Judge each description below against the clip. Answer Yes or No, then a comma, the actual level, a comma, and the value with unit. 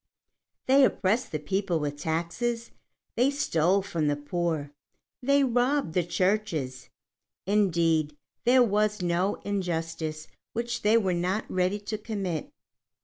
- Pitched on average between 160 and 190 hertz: Yes, medium, 185 Hz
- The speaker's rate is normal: No, slow, 125 wpm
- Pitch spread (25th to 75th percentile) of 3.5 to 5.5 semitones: Yes, average, 5.1 semitones